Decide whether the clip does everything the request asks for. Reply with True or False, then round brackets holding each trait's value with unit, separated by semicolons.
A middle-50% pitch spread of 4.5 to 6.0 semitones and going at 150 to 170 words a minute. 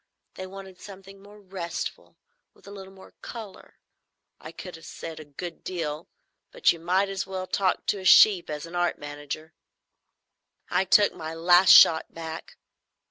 False (3.0 semitones; 165 wpm)